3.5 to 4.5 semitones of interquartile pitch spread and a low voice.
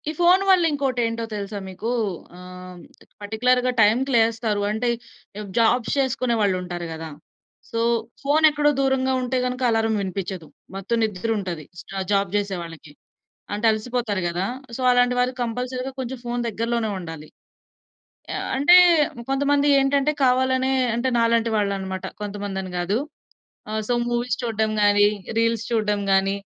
No: average, 4.2 semitones; high, 230 Hz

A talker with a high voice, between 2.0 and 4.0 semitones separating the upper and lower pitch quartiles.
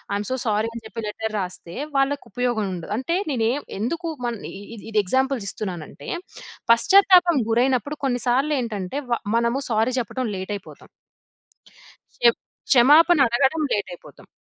No: high, 240 Hz; average, 4.4 semitones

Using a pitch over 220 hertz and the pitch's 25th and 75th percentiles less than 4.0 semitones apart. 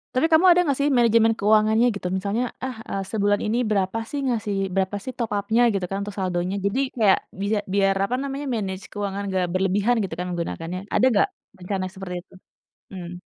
No: high, 200 Hz; average, 3.2 semitones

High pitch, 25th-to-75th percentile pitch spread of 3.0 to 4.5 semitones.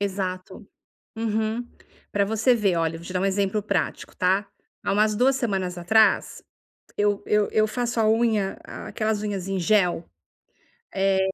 No: high, 205 Hz; narrow, 2.4 semitones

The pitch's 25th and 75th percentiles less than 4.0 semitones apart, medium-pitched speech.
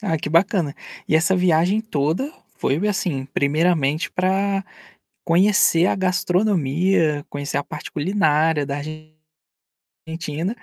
No: average, 4.3 semitones; medium, 170 Hz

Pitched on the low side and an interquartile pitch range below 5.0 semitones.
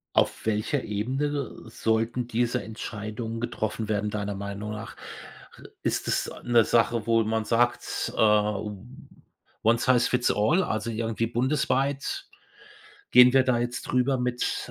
Yes: low, 115 Hz; narrow, 2.6 semitones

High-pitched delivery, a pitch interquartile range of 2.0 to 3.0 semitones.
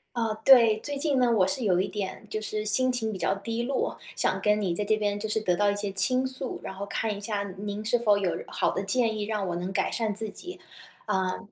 Yes: high, 215 Hz; narrow, 2.5 semitones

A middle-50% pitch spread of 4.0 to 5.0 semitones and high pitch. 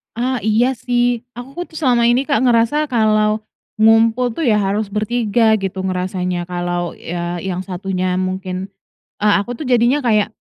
Yes: average, 4.5 semitones; high, 215 Hz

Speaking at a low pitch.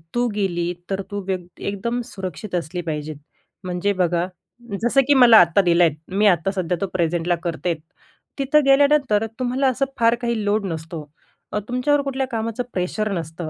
No: high, 200 Hz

